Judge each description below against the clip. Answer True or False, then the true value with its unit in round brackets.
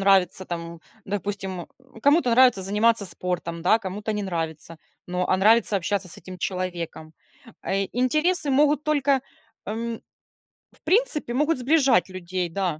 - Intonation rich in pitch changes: True (5.8 semitones)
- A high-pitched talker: True (200 Hz)